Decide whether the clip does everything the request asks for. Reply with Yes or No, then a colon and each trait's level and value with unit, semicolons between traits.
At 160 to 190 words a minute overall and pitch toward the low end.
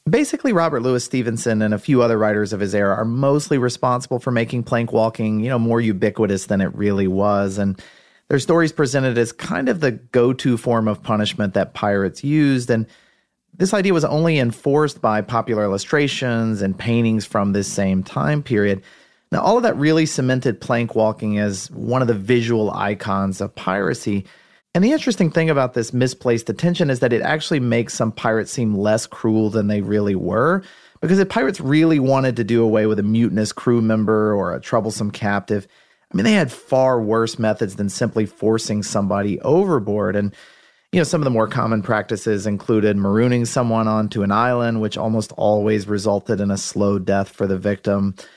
Yes: average, 185 wpm; low, 115 Hz